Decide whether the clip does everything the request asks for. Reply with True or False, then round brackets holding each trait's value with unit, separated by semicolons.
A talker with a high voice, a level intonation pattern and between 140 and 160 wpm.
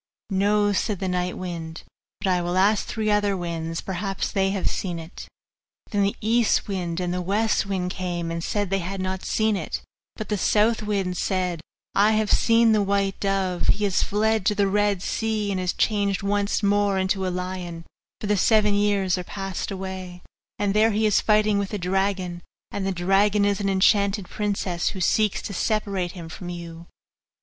False (195 Hz; 2.2 semitones; 195 wpm)